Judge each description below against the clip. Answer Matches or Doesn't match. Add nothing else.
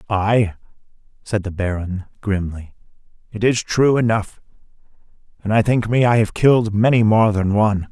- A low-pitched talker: Matches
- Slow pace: Doesn't match